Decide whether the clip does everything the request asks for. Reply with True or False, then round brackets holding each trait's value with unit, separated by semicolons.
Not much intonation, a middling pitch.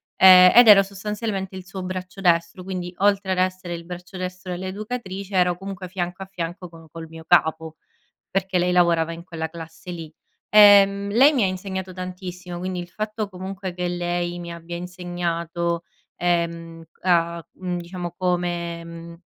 True (1.8 semitones; 180 Hz)